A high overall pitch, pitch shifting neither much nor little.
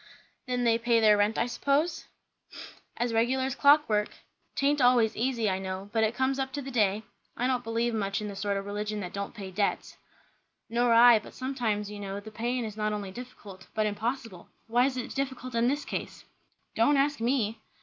Yes: high, 230 Hz; average, 3.4 semitones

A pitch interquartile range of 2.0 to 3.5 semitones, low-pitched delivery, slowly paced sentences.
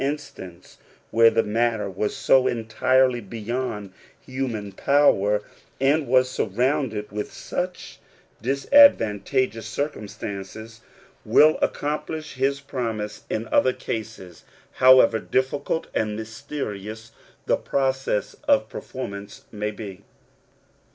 No: average, 4.1 semitones; low, 115 Hz; slow, 100 wpm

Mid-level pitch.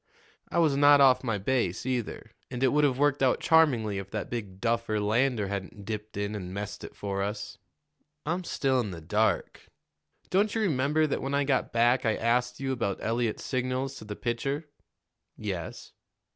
No: low, 120 Hz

